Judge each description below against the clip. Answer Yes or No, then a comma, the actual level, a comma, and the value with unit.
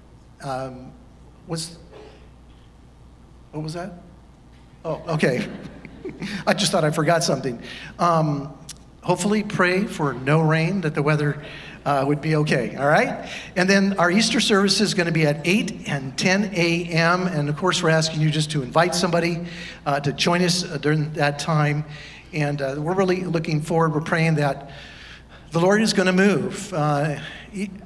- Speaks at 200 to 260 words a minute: No, average, 165 wpm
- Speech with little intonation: No, average, 3.7 semitones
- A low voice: No, medium, 160 Hz